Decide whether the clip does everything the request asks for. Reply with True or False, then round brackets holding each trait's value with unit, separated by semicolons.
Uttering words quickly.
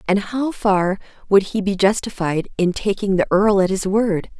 False (190 wpm)